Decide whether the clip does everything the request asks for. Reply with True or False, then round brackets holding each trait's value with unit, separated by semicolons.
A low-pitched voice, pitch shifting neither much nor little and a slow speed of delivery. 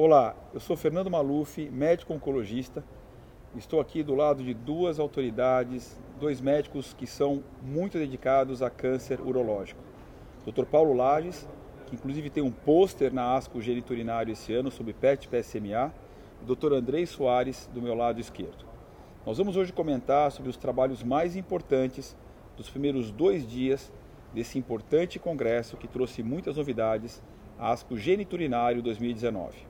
False (130 Hz; 3.6 semitones; 145 wpm)